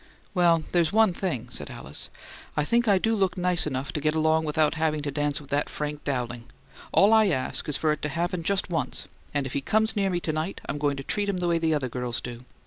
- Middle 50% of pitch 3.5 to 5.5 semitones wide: Yes, average, 4.1 semitones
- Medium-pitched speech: Yes, medium, 155 Hz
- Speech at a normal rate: No, fast, 250 wpm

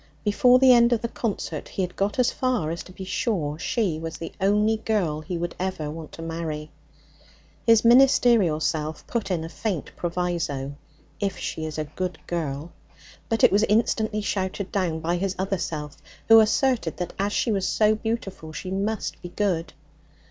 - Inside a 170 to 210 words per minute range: Yes, average, 185 wpm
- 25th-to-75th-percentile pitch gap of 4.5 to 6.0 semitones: Yes, average, 5.0 semitones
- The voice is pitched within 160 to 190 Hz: Yes, medium, 185 Hz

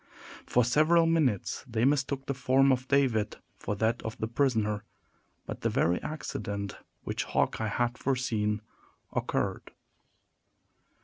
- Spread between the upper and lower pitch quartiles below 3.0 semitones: No, average, 4.0 semitones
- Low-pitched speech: Yes, low, 120 Hz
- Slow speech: Yes, slow, 125 wpm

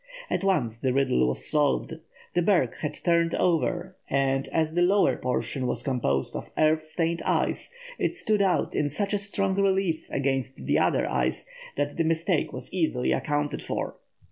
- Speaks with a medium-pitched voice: Yes, medium, 160 Hz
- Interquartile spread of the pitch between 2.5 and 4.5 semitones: No, average, 5.1 semitones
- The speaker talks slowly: No, average, 170 wpm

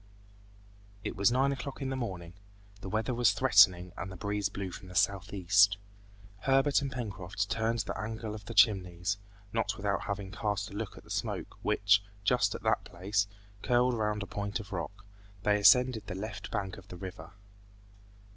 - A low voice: Yes, low, 105 Hz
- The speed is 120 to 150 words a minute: No, average, 180 wpm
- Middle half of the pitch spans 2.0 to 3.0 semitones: Yes, average, 2.7 semitones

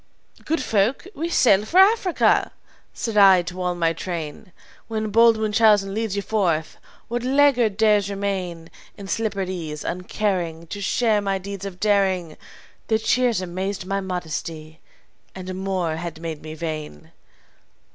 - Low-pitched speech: No, high, 195 Hz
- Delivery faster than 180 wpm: No, average, 145 wpm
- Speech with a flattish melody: No, average, 3.9 semitones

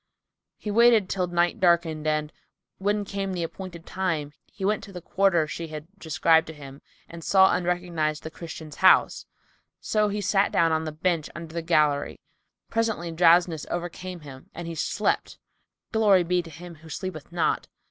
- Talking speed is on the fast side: No, average, 175 wpm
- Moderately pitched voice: Yes, medium, 170 Hz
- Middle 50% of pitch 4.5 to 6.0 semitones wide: No, average, 3.0 semitones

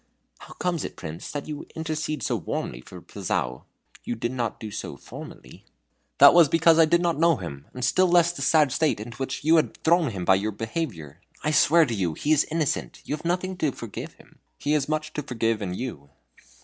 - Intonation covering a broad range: Yes, wide, 6.8 semitones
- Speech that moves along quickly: Yes, fast, 220 wpm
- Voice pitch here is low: No, medium, 145 Hz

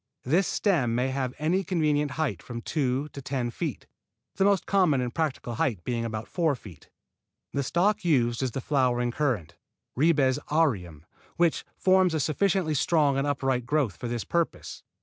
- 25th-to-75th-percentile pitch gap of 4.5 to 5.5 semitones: Yes, average, 5.0 semitones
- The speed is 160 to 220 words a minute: Yes, average, 170 wpm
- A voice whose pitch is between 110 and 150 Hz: Yes, medium, 140 Hz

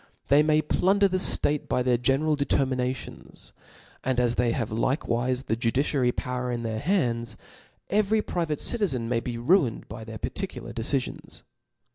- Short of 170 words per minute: Yes, average, 155 wpm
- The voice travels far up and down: No, average, 4.3 semitones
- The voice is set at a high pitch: No, low, 130 Hz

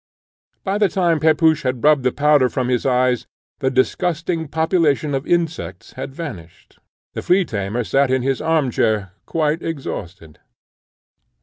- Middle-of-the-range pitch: Yes, medium, 145 Hz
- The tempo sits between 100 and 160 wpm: Yes, average, 145 wpm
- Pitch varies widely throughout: No, average, 4.2 semitones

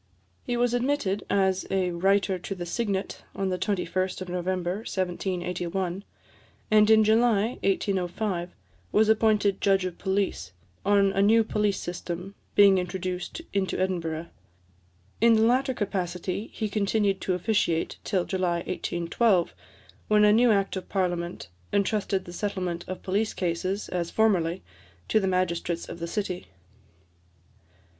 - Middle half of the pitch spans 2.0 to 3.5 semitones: Yes, average, 2.7 semitones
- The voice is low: No, high, 190 Hz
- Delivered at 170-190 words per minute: No, slow, 135 wpm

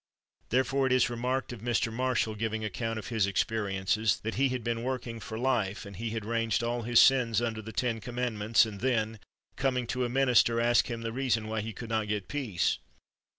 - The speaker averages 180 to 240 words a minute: Yes, fast, 205 wpm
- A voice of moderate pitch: No, low, 115 Hz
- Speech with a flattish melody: Yes, narrow, 2.2 semitones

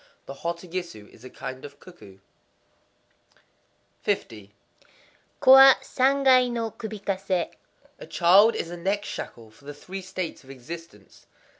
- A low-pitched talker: No, medium, 175 Hz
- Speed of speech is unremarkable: No, slow, 125 wpm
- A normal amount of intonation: No, wide, 7.1 semitones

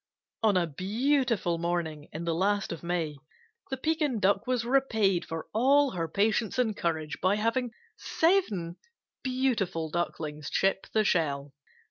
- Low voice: No, high, 195 Hz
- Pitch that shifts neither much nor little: No, wide, 6.8 semitones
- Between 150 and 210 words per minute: No, average, 140 wpm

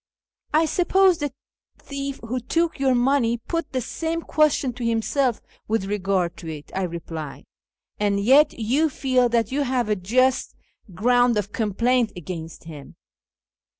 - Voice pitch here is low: No, high, 240 Hz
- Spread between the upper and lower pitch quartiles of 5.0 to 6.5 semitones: Yes, wide, 5.6 semitones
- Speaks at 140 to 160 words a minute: Yes, average, 155 wpm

